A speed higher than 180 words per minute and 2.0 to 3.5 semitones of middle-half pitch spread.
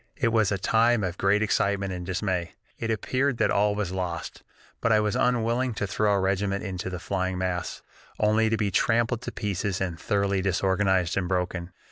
Yes: average, 190 wpm; average, 2.8 semitones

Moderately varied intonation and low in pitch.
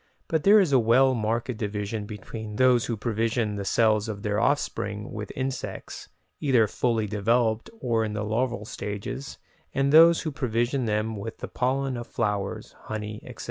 Yes: average, 3.3 semitones; low, 115 Hz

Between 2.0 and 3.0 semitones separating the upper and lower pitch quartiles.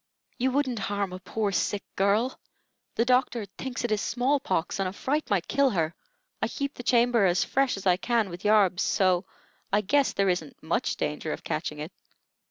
No: average, 5.0 semitones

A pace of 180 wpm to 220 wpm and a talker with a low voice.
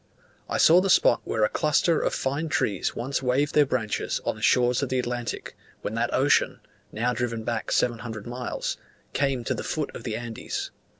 Yes: average, 190 wpm; low, 125 Hz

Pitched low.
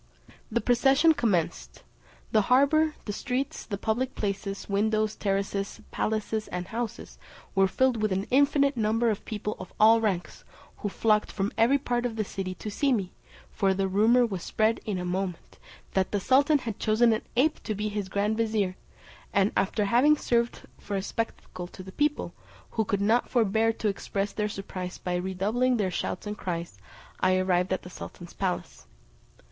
No: high, 210 Hz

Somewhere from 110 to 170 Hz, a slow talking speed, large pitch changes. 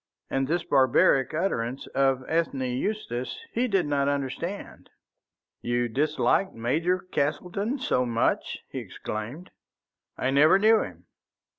Yes: medium, 140 Hz; slow, 120 wpm; wide, 6.1 semitones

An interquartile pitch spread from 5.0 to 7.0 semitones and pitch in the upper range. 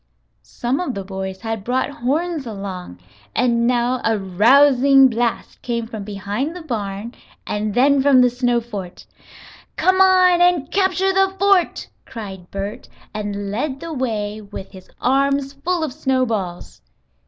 Yes: wide, 5.4 semitones; high, 245 Hz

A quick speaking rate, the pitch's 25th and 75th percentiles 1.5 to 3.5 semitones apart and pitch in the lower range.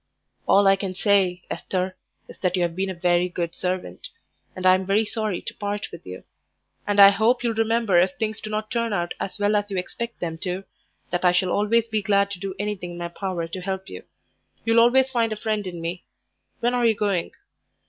No: fast, 220 wpm; average, 3.1 semitones; high, 195 Hz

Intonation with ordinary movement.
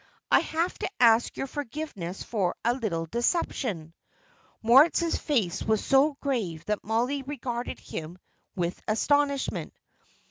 No: wide, 6.3 semitones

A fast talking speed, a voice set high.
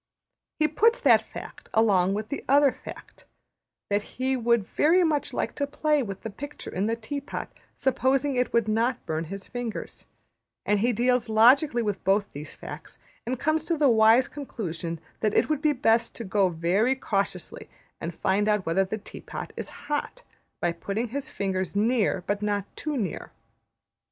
No: average, 180 wpm; high, 225 Hz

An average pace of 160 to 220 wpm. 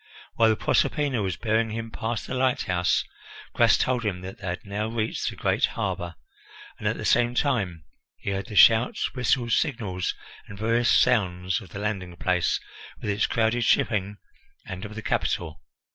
Yes: average, 175 wpm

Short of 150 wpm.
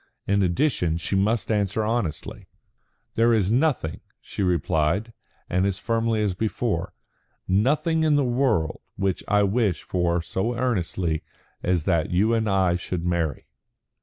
Yes: average, 140 wpm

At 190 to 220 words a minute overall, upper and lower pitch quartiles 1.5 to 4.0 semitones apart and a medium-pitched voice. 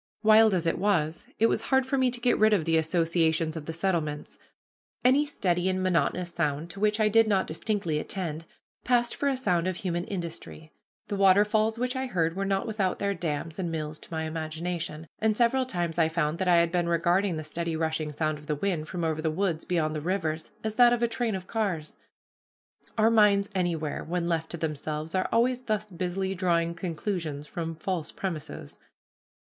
No: average, 200 wpm; average, 4.4 semitones; medium, 175 Hz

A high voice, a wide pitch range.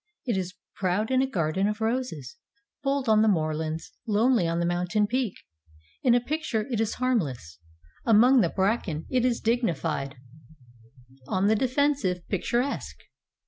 Yes: high, 215 Hz; wide, 6.2 semitones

